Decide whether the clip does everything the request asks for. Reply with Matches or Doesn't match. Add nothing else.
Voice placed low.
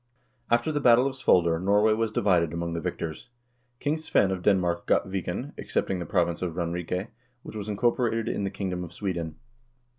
Matches